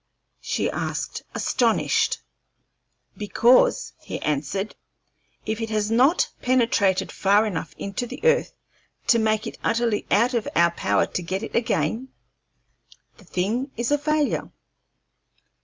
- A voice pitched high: Yes, high, 225 Hz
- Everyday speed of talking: No, slow, 125 wpm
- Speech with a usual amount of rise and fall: Yes, average, 3.6 semitones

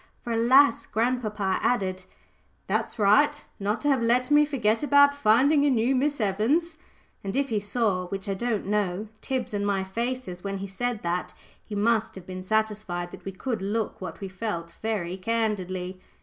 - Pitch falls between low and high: No, high, 215 Hz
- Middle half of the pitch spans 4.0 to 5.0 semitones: Yes, average, 4.4 semitones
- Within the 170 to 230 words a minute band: Yes, average, 180 wpm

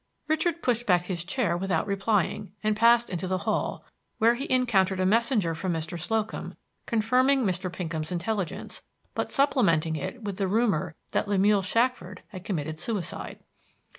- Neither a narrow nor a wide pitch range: Yes, average, 4.7 semitones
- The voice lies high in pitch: Yes, high, 200 Hz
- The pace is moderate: Yes, average, 155 wpm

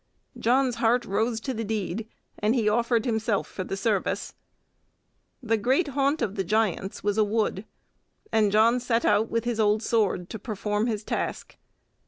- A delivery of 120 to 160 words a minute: No, average, 170 wpm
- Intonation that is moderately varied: No, narrow, 2.2 semitones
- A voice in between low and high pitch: No, high, 220 Hz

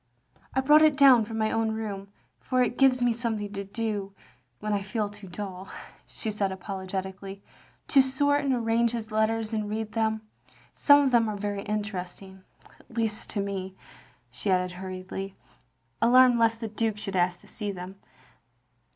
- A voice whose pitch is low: No, high, 215 Hz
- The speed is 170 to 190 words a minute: Yes, average, 175 wpm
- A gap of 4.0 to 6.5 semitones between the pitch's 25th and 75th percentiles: No, average, 3.0 semitones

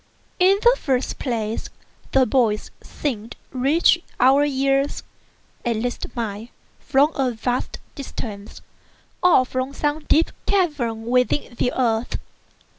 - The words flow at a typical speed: No, slow, 115 wpm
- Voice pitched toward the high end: Yes, very high, 255 Hz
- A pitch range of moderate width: Yes, average, 3.7 semitones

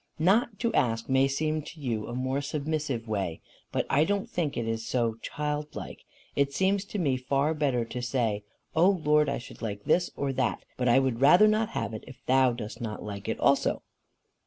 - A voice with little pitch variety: No, average, 4.6 semitones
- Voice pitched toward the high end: No, low, 135 Hz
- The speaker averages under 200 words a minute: No, fast, 205 wpm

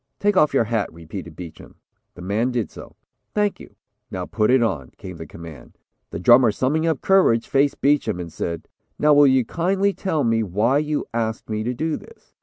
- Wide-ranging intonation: Yes, wide, 7.6 semitones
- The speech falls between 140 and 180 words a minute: No, average, 200 wpm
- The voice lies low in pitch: Yes, low, 120 Hz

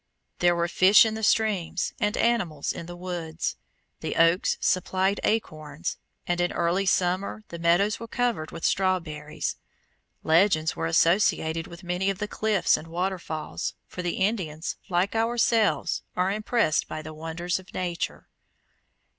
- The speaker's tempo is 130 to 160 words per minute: Yes, average, 145 wpm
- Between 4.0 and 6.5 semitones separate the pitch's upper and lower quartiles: No, average, 3.4 semitones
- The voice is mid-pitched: Yes, medium, 180 Hz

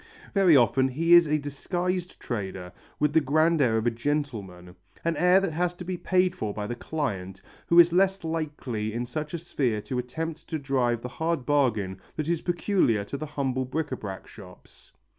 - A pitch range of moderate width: No, wide, 6.0 semitones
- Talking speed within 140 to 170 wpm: No, average, 200 wpm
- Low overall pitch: No, medium, 145 Hz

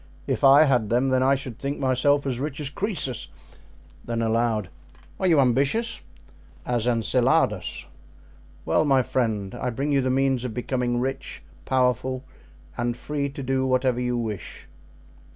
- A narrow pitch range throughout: Yes, narrow, 2.3 semitones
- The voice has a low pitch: Yes, low, 130 Hz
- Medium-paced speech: Yes, average, 150 wpm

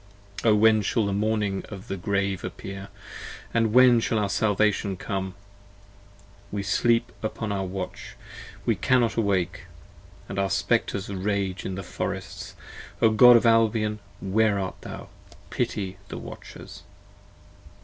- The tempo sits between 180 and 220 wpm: No, slow, 135 wpm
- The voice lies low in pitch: Yes, low, 100 Hz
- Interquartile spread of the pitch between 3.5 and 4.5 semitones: No, narrow, 2.4 semitones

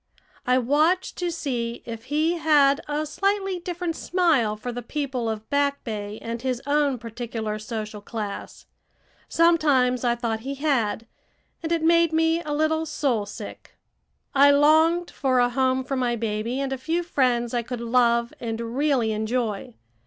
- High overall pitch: Yes, very high, 260 Hz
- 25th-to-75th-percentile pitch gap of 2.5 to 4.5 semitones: No, average, 4.9 semitones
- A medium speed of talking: Yes, average, 160 wpm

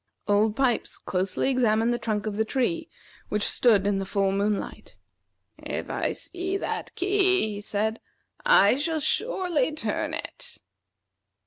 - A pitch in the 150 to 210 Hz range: No, high, 225 Hz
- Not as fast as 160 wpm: Yes, average, 140 wpm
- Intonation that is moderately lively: No, wide, 7.8 semitones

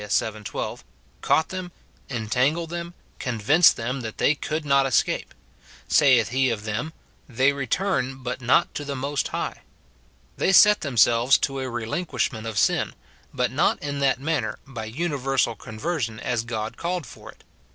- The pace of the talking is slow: No, average, 165 wpm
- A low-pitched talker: Yes, low, 130 Hz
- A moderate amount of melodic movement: Yes, average, 4.5 semitones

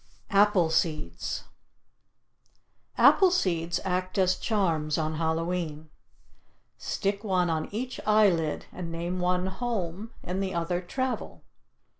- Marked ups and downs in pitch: No, average, 3.1 semitones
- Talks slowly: Yes, slow, 110 wpm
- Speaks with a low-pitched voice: No, medium, 180 Hz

